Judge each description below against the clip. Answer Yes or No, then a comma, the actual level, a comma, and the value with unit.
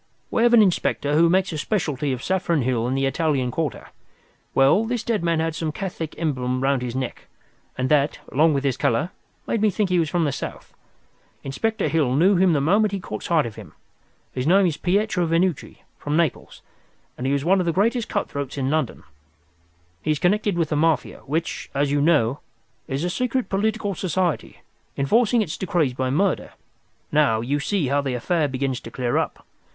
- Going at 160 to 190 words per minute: No, average, 200 wpm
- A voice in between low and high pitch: Yes, medium, 160 Hz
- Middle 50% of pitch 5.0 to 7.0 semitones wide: Yes, wide, 5.4 semitones